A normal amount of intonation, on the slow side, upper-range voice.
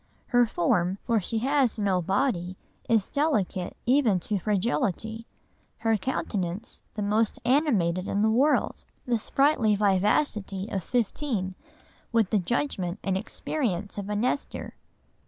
Yes: average, 4.2 semitones; slow, 130 wpm; high, 215 Hz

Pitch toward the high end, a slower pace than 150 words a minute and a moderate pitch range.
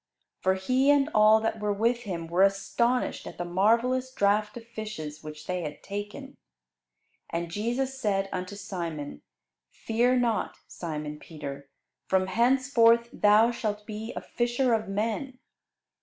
Yes: high, 210 Hz; average, 140 wpm; average, 4.4 semitones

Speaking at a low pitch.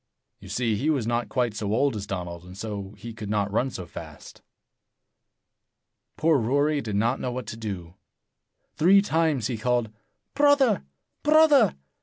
Yes: low, 120 Hz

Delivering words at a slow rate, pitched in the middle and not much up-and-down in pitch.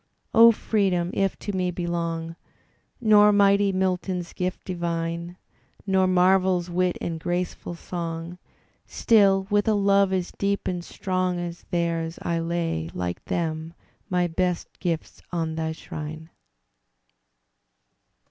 Yes: slow, 120 wpm; medium, 180 Hz; narrow, 2.2 semitones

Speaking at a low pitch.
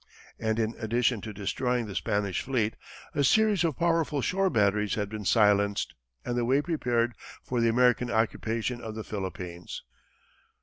Yes: low, 115 Hz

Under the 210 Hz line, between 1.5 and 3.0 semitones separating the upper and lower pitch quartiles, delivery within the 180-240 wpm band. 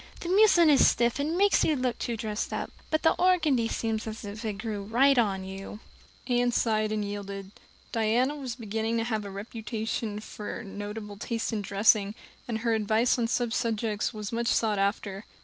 No: high, 225 Hz; average, 2.7 semitones; average, 185 wpm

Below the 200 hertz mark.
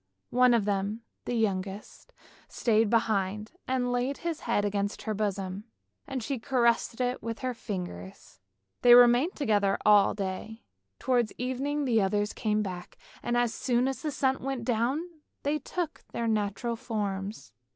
No: high, 230 Hz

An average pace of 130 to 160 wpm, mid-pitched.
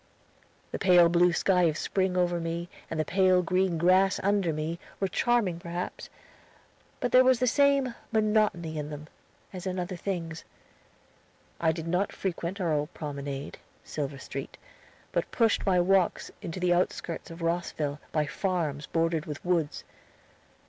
Yes: average, 155 wpm; medium, 175 Hz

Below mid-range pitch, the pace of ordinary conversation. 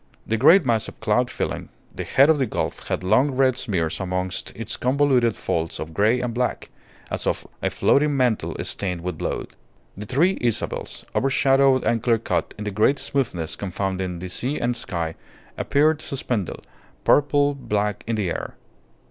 Yes: low, 115 Hz; average, 170 wpm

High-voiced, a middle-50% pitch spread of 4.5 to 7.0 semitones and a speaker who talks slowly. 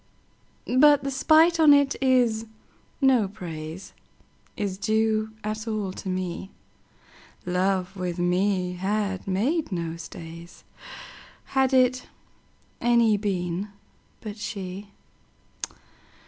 Yes: high, 205 Hz; average, 4.9 semitones; slow, 90 wpm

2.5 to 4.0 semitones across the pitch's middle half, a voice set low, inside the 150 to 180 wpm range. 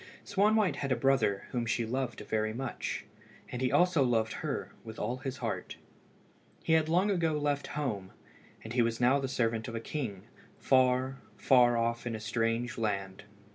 Yes: average, 3.4 semitones; low, 125 Hz; average, 175 wpm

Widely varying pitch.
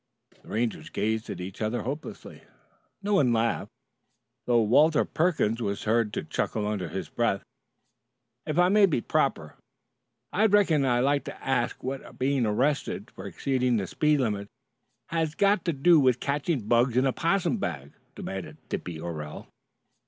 Yes: wide, 6.0 semitones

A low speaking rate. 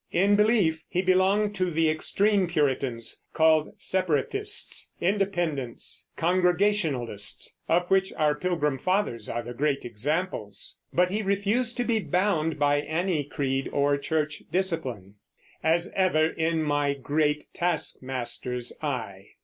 Yes: slow, 125 wpm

